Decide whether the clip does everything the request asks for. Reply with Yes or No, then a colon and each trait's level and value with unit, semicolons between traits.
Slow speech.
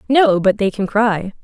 No: fast, 210 wpm